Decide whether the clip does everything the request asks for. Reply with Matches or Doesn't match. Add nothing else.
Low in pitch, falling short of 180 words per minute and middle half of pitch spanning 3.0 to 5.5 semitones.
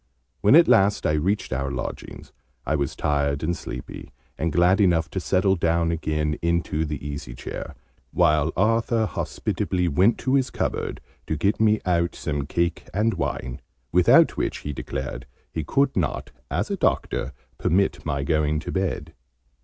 Matches